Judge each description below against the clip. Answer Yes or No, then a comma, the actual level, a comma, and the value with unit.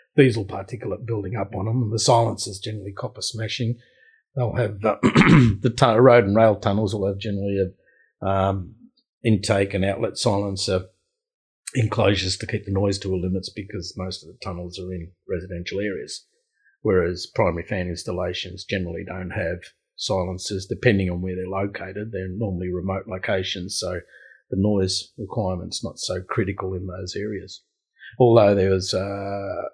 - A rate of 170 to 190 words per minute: No, average, 155 wpm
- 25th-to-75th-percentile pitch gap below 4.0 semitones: Yes, average, 3.5 semitones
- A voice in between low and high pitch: No, low, 100 Hz